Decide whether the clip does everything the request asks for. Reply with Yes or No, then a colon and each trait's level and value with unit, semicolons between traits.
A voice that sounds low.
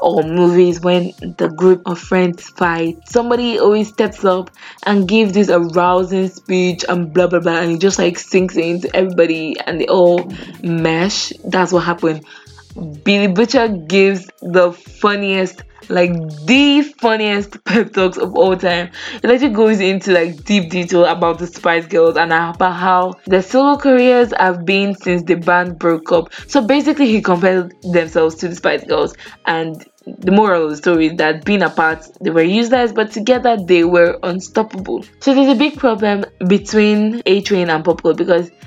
No: medium, 185 Hz